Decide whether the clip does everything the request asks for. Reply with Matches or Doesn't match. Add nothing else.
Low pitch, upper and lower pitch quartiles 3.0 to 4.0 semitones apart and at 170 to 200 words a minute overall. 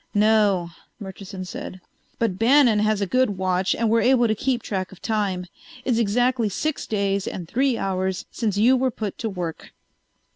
Doesn't match